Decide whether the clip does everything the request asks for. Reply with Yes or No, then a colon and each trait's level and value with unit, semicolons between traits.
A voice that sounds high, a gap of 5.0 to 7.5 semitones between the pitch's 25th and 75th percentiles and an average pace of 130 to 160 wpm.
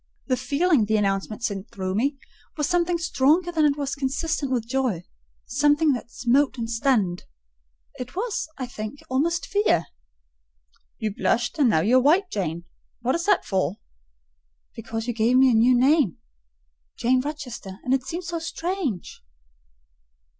Yes: very high, 255 Hz; wide, 5.6 semitones; average, 145 wpm